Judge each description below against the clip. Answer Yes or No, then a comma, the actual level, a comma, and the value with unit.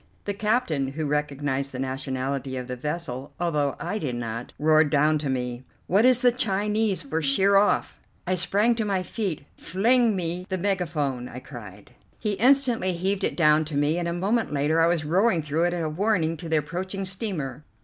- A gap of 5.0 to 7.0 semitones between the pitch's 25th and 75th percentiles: Yes, wide, 5.6 semitones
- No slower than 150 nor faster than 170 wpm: No, average, 190 wpm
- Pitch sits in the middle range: Yes, medium, 165 Hz